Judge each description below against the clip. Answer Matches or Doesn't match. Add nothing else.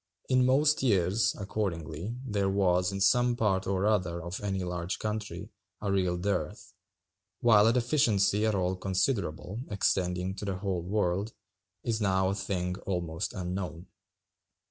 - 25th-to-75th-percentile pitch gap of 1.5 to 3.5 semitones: Matches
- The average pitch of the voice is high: Doesn't match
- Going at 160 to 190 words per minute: Doesn't match